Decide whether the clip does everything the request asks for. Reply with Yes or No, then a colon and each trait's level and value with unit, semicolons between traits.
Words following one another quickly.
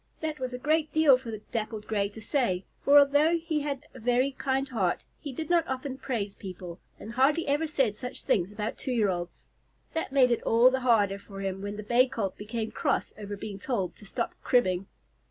Yes: fast, 215 wpm